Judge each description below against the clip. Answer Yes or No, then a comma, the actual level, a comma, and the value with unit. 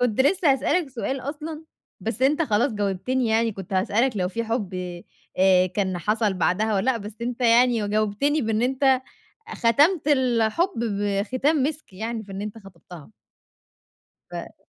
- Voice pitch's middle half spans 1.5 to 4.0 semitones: No, average, 4.5 semitones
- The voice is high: Yes, high, 230 Hz